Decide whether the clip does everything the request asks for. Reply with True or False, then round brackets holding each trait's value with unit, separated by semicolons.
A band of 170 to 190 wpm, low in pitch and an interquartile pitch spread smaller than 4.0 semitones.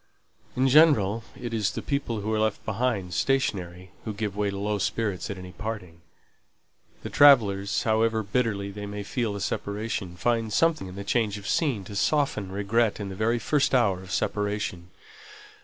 True (175 wpm; 105 Hz; 2.8 semitones)